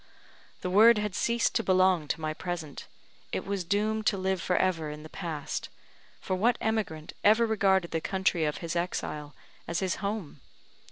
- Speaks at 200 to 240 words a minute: No, average, 175 wpm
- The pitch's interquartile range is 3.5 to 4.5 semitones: Yes, average, 4.1 semitones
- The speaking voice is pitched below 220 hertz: Yes, medium, 185 Hz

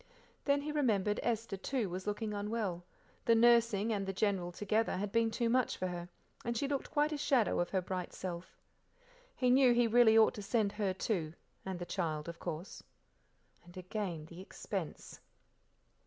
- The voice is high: Yes, high, 210 Hz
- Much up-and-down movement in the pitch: No, average, 4.2 semitones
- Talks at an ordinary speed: Yes, average, 180 wpm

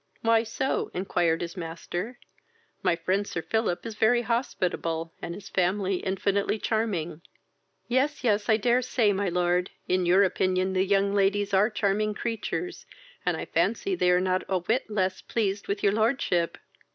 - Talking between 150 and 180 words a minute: Yes, average, 165 wpm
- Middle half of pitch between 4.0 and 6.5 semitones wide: No, average, 3.5 semitones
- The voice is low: No, high, 200 Hz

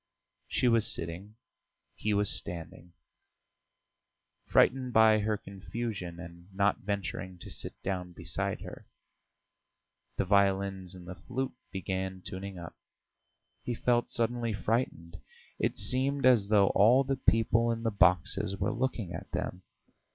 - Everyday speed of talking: No, slow, 130 wpm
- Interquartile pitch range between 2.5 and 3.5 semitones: No, average, 4.0 semitones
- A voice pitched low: Yes, low, 100 Hz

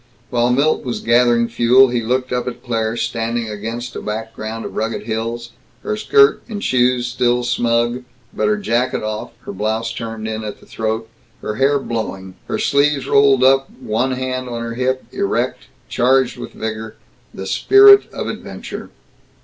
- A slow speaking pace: No, average, 165 wpm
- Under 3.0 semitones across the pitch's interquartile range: Yes, narrow, 2.4 semitones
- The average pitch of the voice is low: Yes, low, 120 Hz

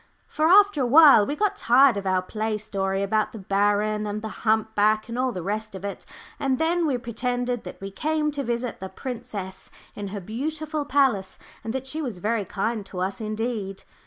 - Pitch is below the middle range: No, high, 220 Hz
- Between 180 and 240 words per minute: Yes, average, 200 wpm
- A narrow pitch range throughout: No, average, 4.8 semitones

